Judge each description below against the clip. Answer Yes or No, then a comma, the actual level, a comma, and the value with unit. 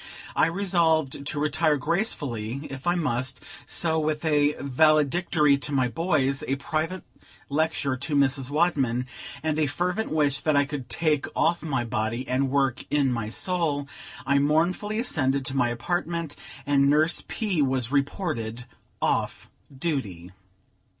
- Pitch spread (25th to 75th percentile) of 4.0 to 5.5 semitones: No, average, 3.3 semitones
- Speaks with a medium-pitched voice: Yes, medium, 145 Hz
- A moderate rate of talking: Yes, average, 145 wpm